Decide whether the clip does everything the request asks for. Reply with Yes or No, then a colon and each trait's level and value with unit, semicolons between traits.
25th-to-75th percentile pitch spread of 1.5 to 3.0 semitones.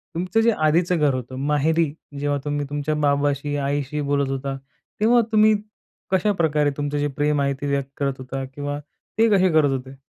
Yes: narrow, 2.5 semitones